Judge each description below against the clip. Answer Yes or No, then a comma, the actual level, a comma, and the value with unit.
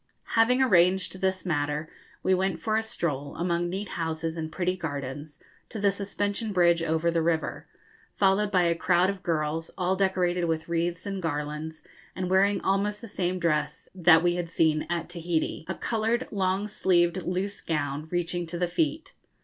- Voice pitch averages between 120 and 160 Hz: No, medium, 175 Hz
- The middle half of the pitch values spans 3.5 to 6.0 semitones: No, average, 2.9 semitones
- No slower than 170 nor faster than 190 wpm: Yes, average, 175 wpm